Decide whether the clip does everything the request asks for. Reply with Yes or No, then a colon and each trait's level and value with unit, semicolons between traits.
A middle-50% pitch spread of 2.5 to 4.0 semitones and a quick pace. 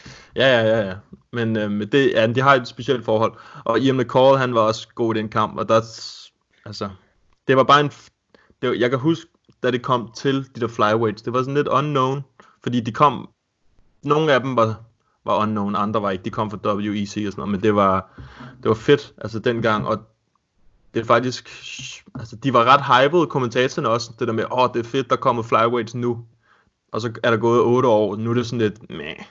Yes: average, 2.9 semitones; fast, 235 wpm